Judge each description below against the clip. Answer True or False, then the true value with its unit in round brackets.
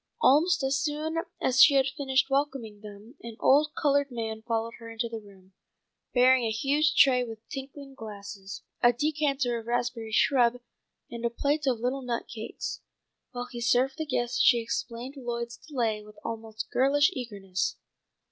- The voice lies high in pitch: True (245 Hz)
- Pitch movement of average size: True (3.4 semitones)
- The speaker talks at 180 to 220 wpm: False (165 wpm)